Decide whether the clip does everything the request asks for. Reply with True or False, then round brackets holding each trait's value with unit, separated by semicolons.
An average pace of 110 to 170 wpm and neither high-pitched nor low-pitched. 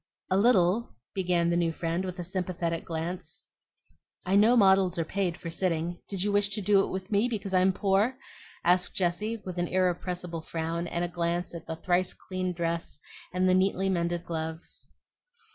False (180 wpm; 180 Hz)